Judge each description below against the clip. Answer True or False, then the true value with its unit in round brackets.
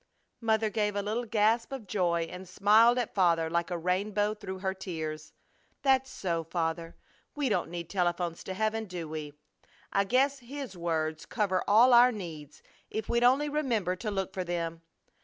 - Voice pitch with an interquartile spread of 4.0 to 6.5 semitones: True (4.7 semitones)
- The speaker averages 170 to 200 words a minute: True (175 wpm)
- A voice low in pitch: False (195 Hz)